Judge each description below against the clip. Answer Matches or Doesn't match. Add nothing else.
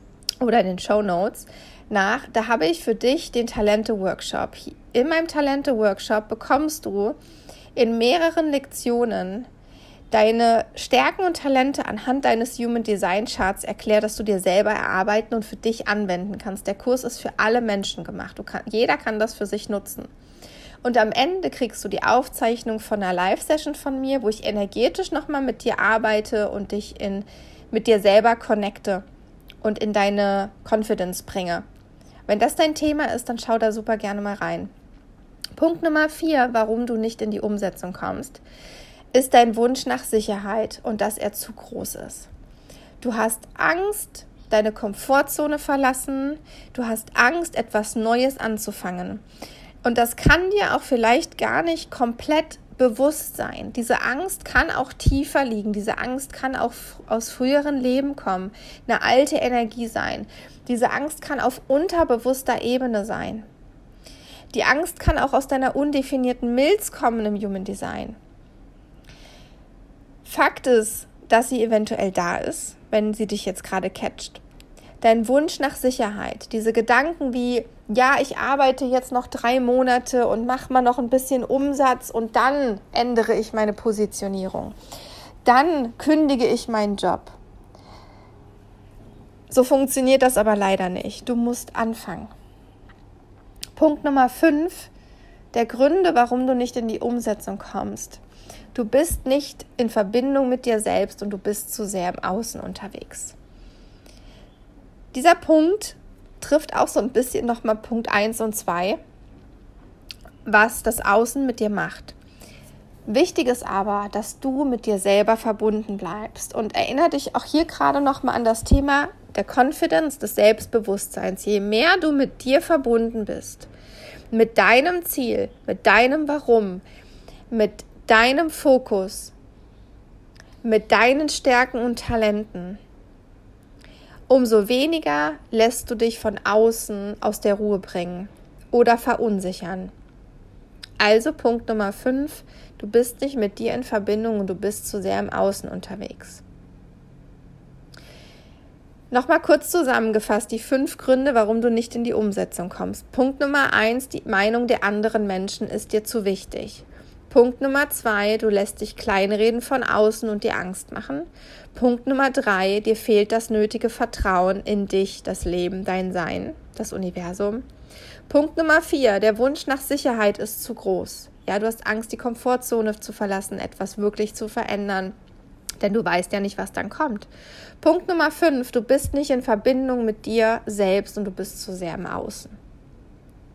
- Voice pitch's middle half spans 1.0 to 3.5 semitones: Doesn't match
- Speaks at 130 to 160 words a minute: Matches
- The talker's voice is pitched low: Doesn't match